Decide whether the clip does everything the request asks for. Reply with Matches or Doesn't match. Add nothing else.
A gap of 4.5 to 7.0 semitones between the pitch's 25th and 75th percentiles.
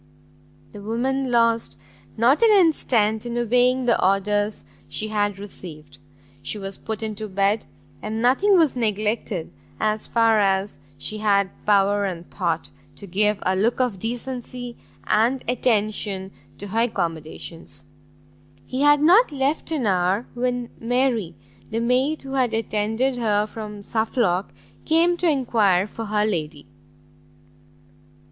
Doesn't match